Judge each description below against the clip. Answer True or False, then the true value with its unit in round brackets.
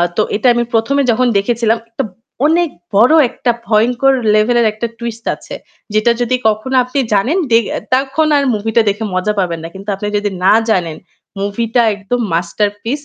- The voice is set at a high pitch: True (225 Hz)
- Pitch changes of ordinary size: True (3.2 semitones)